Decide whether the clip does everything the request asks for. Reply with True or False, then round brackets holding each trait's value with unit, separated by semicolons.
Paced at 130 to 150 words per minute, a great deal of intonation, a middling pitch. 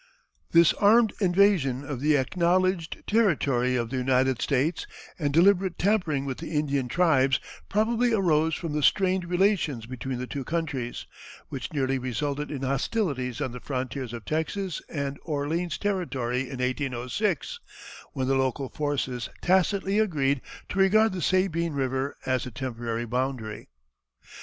True (140 wpm; 5.7 semitones; 145 Hz)